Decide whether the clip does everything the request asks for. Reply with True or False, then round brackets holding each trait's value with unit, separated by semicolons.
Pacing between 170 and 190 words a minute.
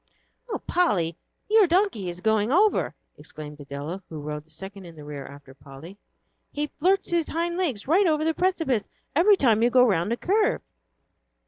True (180 wpm)